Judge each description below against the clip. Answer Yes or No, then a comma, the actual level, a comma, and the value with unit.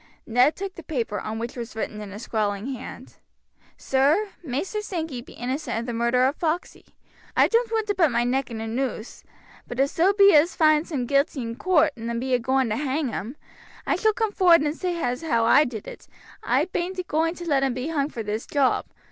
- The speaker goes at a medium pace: No, fast, 225 wpm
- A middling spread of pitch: No, wide, 5.8 semitones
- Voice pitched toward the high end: Yes, very high, 270 Hz